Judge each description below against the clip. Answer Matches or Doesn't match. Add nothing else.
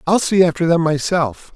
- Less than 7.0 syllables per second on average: Matches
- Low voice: Doesn't match